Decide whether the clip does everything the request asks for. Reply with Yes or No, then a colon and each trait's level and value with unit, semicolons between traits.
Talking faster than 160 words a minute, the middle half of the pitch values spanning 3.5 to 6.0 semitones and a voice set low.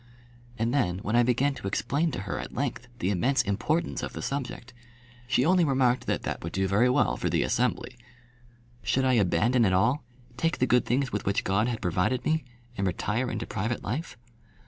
Yes: average, 200 wpm; average, 4.6 semitones; low, 120 Hz